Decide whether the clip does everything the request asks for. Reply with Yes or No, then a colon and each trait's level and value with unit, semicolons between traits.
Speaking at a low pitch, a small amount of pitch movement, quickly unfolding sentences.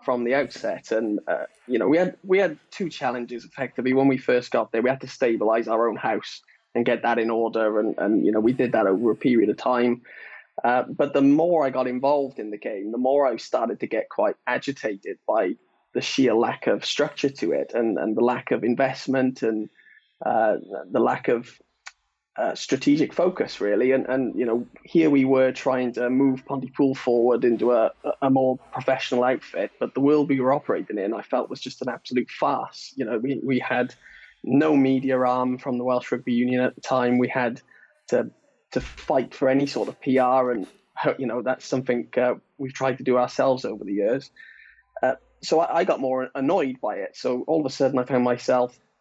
Yes: low, 130 Hz; narrow, 1.8 semitones; fast, 210 wpm